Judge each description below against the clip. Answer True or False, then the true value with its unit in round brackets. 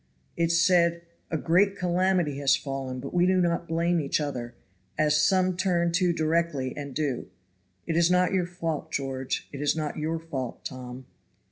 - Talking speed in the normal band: True (170 wpm)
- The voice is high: False (165 Hz)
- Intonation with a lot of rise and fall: False (3.7 semitones)